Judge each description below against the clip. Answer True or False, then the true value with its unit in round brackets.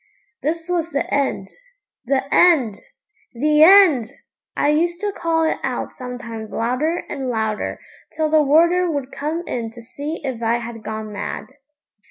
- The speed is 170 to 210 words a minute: False (155 wpm)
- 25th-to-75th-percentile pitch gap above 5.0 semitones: True (5.6 semitones)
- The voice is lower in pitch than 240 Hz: False (280 Hz)